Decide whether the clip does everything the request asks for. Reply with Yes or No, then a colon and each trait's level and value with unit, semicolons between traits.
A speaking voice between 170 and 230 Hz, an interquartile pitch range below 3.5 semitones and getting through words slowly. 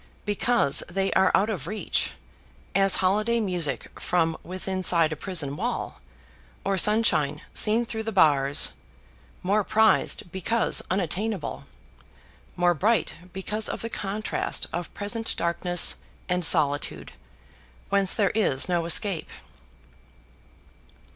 No: high, 190 Hz; average, 3.8 semitones; slow, 115 wpm